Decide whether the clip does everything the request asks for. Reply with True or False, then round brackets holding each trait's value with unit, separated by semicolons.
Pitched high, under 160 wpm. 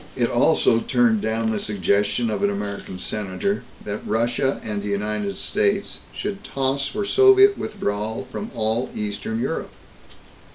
False (110 Hz; 140 wpm)